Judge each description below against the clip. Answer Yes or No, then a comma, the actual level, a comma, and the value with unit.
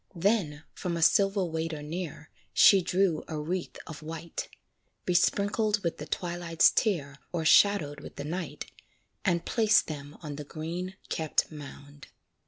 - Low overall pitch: No, medium, 165 Hz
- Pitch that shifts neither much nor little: Yes, average, 3.6 semitones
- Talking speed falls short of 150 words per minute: Yes, average, 140 wpm